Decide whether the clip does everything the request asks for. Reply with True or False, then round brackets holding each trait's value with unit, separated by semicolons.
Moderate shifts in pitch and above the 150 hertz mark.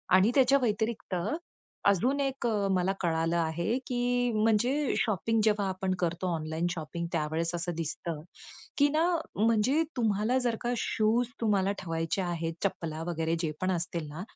False (5.9 semitones; 190 Hz)